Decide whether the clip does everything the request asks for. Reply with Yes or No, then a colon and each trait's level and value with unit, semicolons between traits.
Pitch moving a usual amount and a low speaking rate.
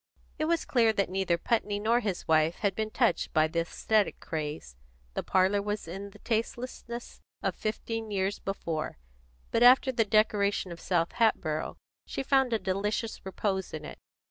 No: average, 4.0 semitones; average, 170 wpm